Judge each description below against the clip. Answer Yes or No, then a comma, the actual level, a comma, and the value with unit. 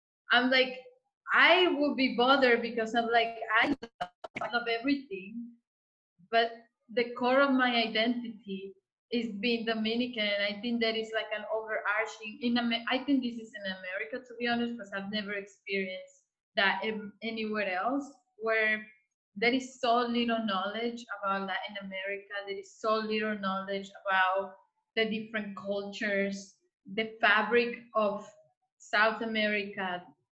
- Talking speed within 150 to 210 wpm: No, slow, 135 wpm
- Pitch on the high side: Yes, high, 220 Hz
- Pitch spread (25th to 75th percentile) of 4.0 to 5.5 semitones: No, average, 3.0 semitones